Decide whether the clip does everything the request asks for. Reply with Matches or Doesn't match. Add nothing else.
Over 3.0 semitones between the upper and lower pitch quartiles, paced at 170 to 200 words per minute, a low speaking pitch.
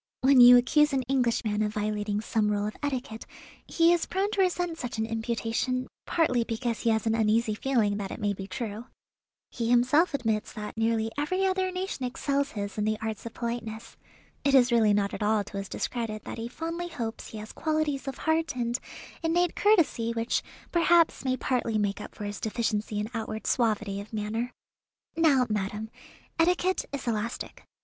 Doesn't match